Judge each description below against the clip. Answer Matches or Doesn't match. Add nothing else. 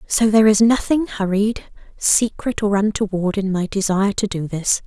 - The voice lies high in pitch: Matches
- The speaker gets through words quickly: Doesn't match